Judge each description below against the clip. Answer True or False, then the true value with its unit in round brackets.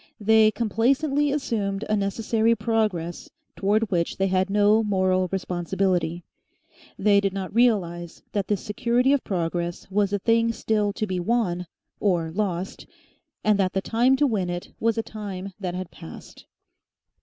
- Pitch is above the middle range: True (200 Hz)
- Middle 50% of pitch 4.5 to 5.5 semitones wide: False (3.3 semitones)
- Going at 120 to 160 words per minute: True (150 wpm)